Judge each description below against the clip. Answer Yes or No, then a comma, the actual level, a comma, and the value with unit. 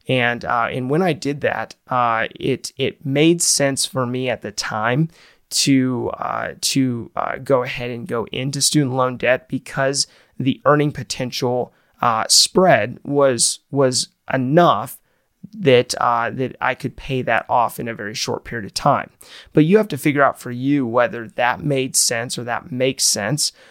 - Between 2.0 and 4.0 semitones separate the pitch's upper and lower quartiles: Yes, average, 2.8 semitones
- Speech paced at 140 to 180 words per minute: Yes, average, 175 wpm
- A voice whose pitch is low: Yes, low, 130 Hz